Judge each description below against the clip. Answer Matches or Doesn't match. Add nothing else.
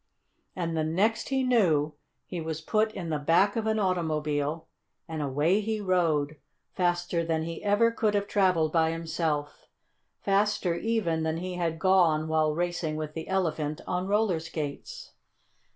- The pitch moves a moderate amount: Matches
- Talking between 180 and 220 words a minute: Doesn't match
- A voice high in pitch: Doesn't match